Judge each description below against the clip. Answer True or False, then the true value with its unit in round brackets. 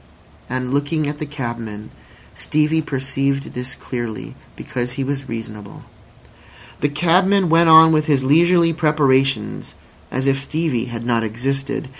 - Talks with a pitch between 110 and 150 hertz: True (135 Hz)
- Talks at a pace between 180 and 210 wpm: False (135 wpm)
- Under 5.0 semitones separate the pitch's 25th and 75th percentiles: True (3.9 semitones)